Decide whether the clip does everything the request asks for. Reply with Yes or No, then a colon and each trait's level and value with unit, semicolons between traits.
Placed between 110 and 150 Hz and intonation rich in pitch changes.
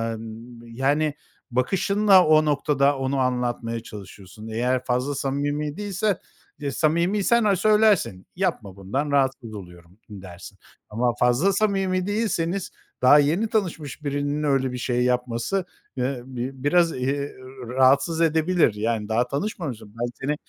Yes: medium, 140 Hz; wide, 5.7 semitones